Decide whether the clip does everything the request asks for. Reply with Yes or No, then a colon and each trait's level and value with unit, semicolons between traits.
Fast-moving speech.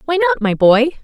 Yes: fast, 230 wpm